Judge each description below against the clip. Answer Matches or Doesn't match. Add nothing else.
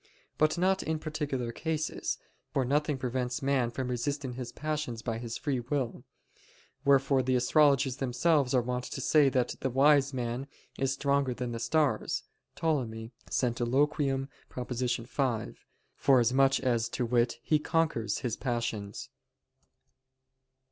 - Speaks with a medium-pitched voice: Doesn't match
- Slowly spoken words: Matches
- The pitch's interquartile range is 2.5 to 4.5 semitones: Matches